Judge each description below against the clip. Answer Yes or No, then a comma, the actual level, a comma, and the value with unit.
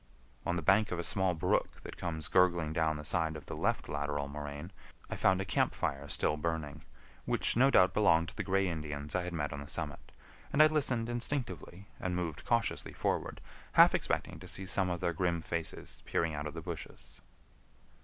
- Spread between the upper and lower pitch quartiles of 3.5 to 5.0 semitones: Yes, average, 4.0 semitones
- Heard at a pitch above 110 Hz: No, very low, 85 Hz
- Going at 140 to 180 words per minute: No, fast, 205 wpm